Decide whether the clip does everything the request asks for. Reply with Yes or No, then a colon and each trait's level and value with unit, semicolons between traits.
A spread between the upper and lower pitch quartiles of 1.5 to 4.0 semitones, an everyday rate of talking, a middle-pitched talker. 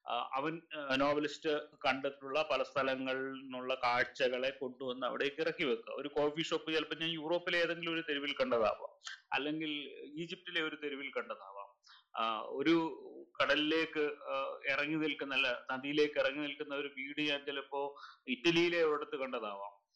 Yes: average, 3.3 semitones; average, 115 wpm; medium, 150 Hz